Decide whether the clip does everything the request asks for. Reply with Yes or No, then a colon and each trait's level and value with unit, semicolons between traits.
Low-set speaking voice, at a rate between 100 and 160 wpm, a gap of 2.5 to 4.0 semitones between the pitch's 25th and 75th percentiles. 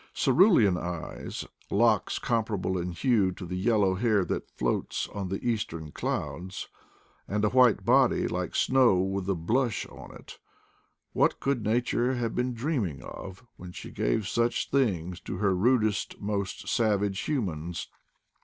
No: low, 105 Hz; average, 150 wpm; average, 4.6 semitones